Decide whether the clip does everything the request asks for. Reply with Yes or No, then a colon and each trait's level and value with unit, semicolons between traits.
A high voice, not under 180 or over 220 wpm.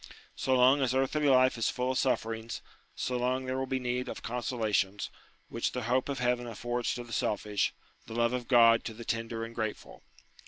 No: low, 120 Hz; average, 200 wpm